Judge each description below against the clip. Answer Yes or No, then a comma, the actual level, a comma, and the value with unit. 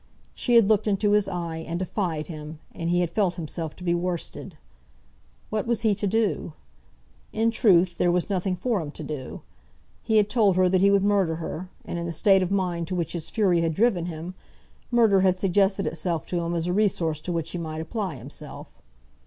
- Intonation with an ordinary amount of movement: Yes, average, 3.3 semitones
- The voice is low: No, medium, 180 Hz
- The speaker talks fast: Yes, fast, 210 wpm